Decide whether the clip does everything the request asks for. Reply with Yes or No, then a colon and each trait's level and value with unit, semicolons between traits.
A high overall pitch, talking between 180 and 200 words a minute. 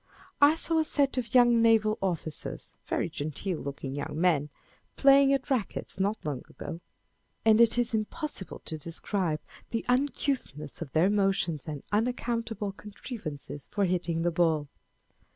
No: high, 200 Hz; average, 150 wpm